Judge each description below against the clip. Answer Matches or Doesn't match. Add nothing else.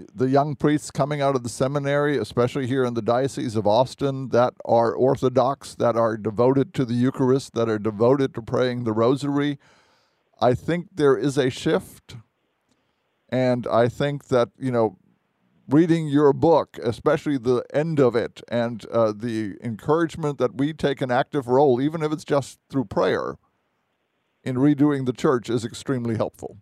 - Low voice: Matches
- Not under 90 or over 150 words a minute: Doesn't match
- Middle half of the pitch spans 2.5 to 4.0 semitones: Matches